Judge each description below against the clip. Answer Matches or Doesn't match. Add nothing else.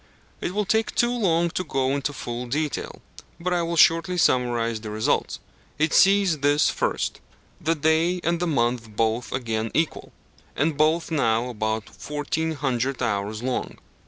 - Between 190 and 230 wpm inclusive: Doesn't match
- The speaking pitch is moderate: Matches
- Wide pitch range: Matches